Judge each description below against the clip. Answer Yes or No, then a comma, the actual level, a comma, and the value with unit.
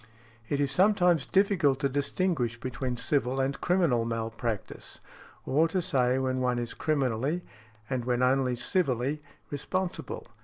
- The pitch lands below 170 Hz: Yes, low, 135 Hz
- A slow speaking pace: Yes, slow, 130 wpm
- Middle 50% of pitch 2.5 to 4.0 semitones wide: No, average, 4.7 semitones